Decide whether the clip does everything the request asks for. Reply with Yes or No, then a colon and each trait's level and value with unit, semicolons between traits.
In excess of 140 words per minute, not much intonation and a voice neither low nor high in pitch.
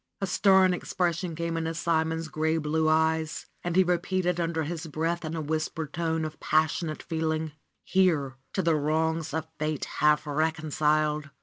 Yes: average, 160 wpm; narrow, 1.4 semitones; medium, 160 Hz